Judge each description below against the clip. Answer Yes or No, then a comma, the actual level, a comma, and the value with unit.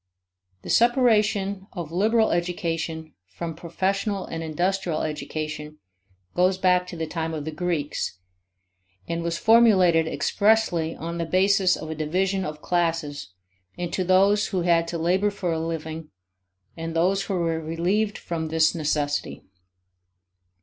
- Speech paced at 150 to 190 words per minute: No, slow, 135 wpm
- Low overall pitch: No, medium, 170 Hz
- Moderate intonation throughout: Yes, average, 3.1 semitones